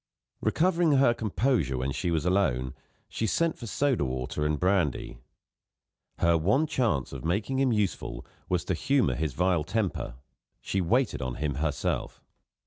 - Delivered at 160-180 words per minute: No, average, 150 wpm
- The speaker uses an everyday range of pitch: No, wide, 8.2 semitones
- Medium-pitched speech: No, very low, 90 Hz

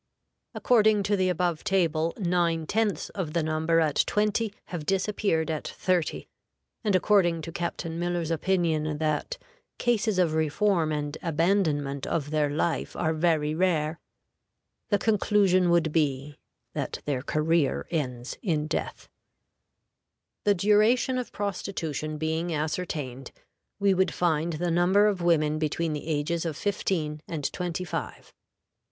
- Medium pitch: Yes, medium, 165 Hz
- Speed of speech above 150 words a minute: No, slow, 135 wpm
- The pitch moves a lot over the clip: No, average, 3.6 semitones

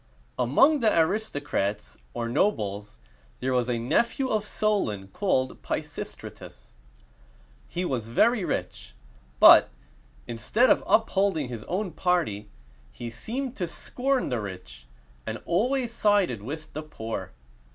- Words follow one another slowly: Yes, slow, 130 wpm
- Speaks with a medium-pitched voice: Yes, medium, 155 Hz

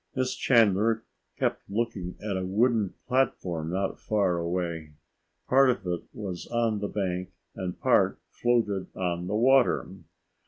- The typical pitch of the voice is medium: No, low, 100 Hz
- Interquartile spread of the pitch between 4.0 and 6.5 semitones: Yes, average, 4.5 semitones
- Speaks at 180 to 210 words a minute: No, slow, 135 wpm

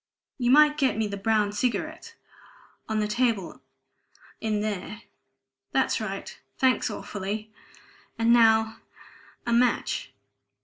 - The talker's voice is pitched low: No, high, 220 Hz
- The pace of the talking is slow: Yes, slow, 115 wpm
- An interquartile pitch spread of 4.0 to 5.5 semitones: No, average, 2.7 semitones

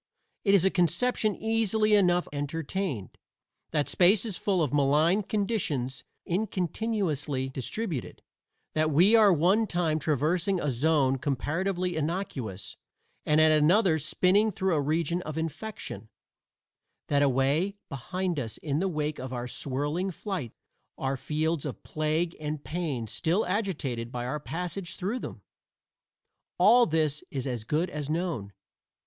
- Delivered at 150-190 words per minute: No, average, 140 wpm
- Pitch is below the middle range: No, medium, 160 Hz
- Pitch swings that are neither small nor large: Yes, average, 4.9 semitones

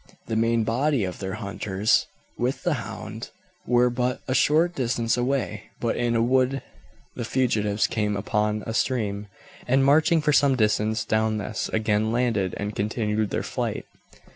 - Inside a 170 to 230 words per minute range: No, average, 160 wpm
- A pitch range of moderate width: Yes, average, 3.1 semitones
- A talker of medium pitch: No, low, 115 Hz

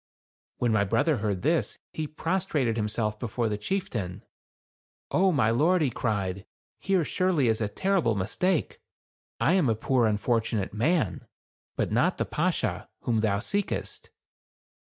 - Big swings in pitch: Yes, wide, 7.6 semitones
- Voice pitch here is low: Yes, low, 115 Hz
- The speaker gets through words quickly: No, average, 150 wpm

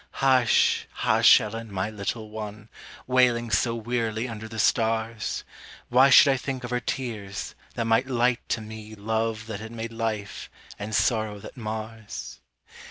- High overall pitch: No, low, 115 Hz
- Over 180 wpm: No, average, 155 wpm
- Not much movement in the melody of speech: Yes, narrow, 1.8 semitones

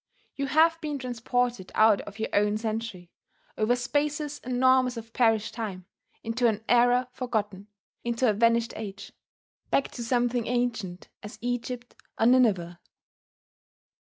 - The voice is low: No, high, 235 Hz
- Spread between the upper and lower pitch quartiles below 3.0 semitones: Yes, narrow, 2.6 semitones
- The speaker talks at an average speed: No, slow, 130 wpm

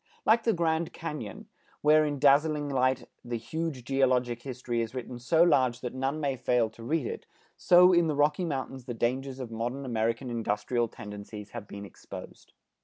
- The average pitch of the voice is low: Yes, low, 130 Hz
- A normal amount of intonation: Yes, average, 4.1 semitones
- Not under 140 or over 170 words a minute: No, average, 180 wpm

